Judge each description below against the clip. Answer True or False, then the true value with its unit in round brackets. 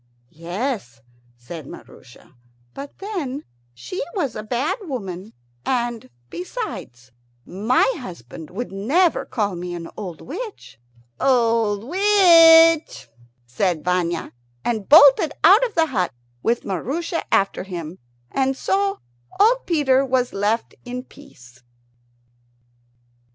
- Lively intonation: True (8.9 semitones)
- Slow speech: True (110 wpm)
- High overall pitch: True (235 Hz)